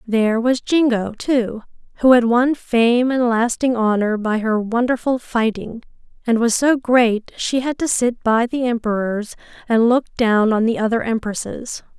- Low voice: No, high, 235 Hz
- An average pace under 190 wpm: Yes, average, 165 wpm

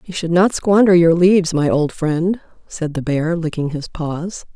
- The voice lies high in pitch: No, medium, 170 Hz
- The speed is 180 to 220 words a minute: Yes, average, 200 wpm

